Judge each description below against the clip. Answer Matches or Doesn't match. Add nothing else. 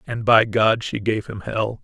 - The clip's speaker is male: Matches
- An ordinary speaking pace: Doesn't match